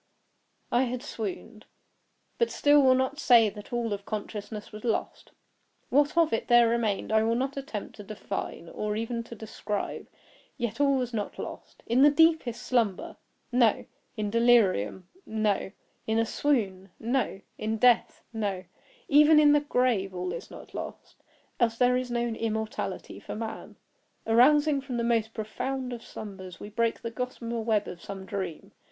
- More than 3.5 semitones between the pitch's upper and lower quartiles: No, average, 3.2 semitones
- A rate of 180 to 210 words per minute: No, average, 155 wpm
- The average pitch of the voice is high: Yes, high, 230 Hz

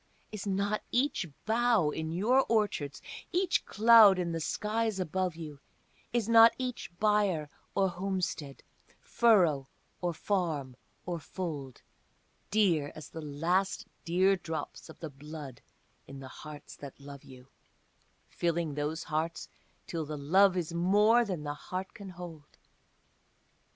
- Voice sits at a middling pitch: Yes, medium, 175 Hz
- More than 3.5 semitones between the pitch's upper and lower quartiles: Yes, average, 5.2 semitones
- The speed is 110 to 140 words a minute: Yes, slow, 135 wpm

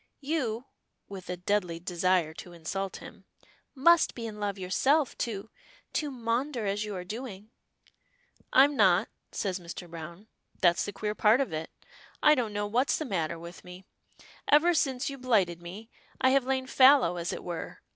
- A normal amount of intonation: No, wide, 6.4 semitones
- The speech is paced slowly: No, average, 170 wpm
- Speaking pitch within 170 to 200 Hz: No, high, 210 Hz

